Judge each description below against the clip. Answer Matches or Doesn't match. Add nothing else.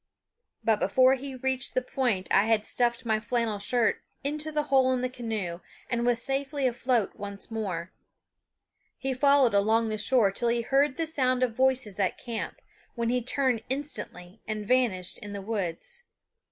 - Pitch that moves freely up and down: Doesn't match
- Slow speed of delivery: Doesn't match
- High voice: Matches